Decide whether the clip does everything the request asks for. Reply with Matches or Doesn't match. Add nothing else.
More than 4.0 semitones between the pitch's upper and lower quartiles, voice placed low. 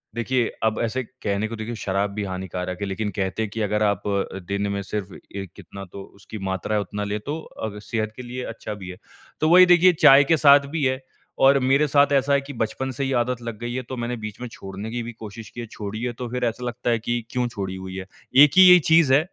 Matches